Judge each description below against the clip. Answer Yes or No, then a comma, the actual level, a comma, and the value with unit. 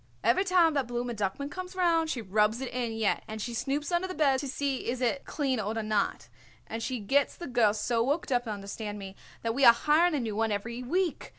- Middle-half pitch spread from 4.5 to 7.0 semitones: Yes, average, 4.8 semitones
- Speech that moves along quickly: Yes, fast, 225 wpm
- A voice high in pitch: Yes, high, 245 Hz